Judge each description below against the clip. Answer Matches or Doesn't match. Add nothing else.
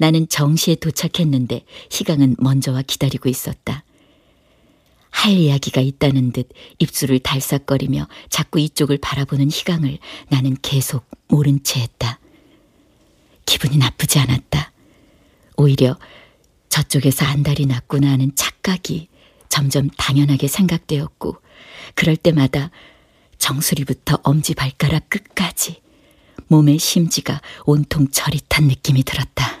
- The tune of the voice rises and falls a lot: Doesn't match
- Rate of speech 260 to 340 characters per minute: Matches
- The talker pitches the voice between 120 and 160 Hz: Matches